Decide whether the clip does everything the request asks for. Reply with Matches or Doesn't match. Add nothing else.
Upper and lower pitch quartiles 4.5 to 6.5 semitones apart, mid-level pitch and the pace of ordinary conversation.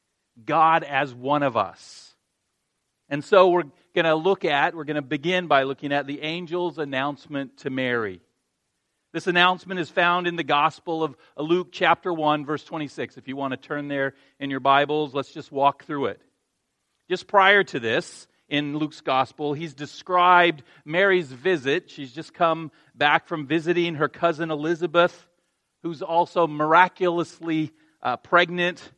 Doesn't match